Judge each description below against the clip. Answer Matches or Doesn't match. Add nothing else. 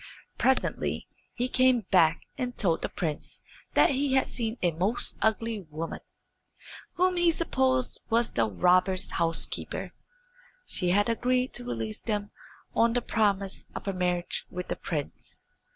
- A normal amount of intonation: Doesn't match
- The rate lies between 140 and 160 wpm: Matches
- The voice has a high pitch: Matches